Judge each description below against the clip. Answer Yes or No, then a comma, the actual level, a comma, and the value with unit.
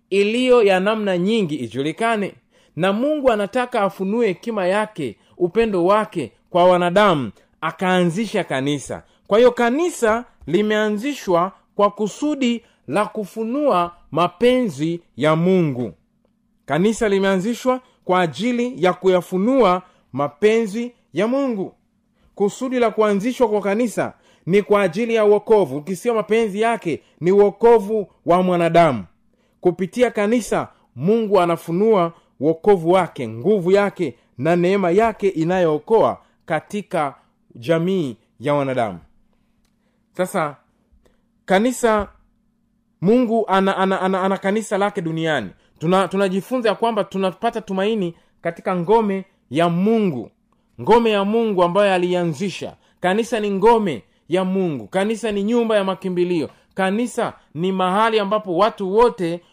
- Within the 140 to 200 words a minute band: No, average, 115 wpm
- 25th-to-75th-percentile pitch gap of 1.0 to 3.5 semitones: No, average, 4.1 semitones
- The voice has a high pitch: Yes, high, 200 Hz